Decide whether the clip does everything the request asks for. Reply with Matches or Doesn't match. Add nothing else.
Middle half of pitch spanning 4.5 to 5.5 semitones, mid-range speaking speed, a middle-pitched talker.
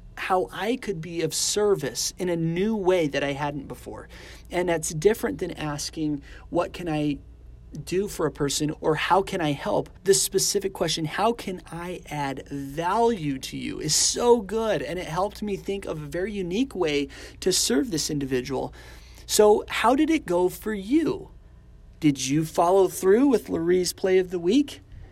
Matches